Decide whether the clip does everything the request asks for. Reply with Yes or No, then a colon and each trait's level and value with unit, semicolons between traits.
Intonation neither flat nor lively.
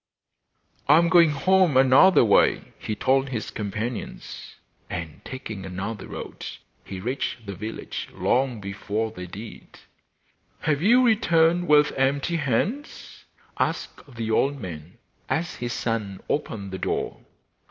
No: wide, 6.5 semitones